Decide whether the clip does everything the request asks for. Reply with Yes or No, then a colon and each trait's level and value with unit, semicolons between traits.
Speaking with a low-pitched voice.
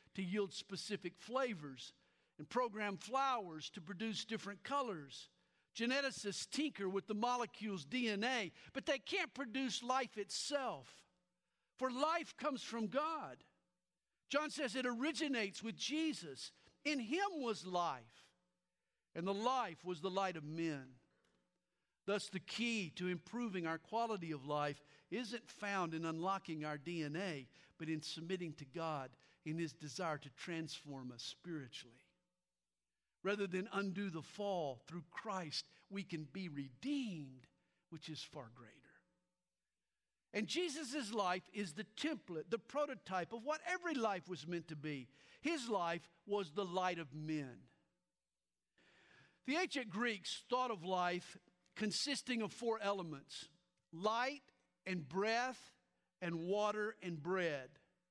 No: high, 195 Hz